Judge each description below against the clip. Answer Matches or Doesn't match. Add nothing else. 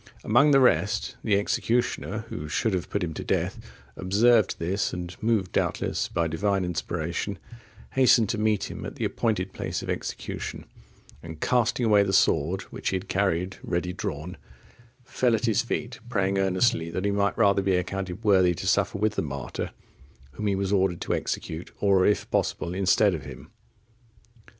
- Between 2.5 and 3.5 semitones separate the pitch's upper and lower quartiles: Matches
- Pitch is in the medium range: Doesn't match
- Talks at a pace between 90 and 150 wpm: Doesn't match